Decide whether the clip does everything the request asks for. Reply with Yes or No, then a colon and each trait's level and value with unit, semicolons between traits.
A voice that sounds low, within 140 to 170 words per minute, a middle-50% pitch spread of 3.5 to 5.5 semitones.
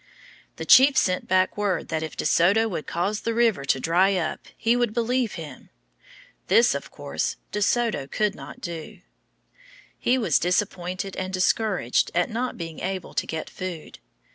No: high, 190 Hz; average, 165 wpm; average, 4.6 semitones